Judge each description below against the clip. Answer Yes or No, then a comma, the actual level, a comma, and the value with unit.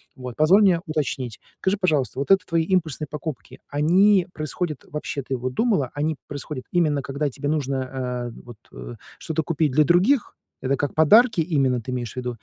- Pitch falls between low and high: Yes, medium, 150 Hz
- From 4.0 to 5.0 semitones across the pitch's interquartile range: Yes, average, 4.5 semitones